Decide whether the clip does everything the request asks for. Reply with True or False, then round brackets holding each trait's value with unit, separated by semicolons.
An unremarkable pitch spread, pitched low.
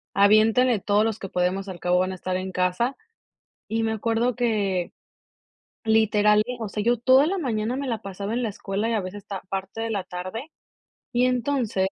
False (3.4 semitones; 215 Hz)